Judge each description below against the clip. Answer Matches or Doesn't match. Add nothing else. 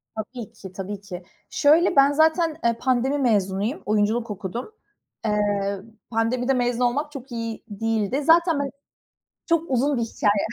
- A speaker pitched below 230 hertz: Doesn't match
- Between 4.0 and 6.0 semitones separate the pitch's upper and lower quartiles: Matches